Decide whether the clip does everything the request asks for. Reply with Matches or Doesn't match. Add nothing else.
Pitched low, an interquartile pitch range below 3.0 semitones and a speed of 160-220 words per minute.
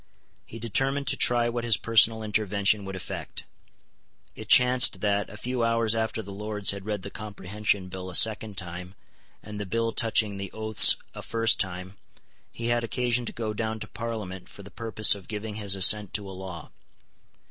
Matches